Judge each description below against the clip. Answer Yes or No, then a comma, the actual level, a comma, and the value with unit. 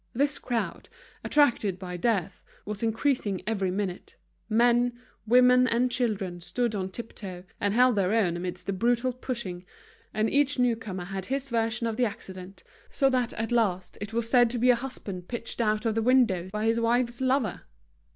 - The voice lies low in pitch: No, high, 225 Hz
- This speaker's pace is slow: No, average, 180 wpm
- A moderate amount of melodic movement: Yes, average, 4.1 semitones